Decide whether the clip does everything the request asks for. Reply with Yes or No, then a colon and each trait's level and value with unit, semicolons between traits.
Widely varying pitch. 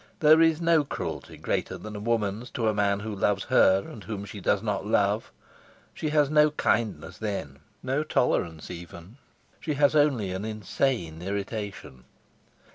Yes: wide, 6.3 semitones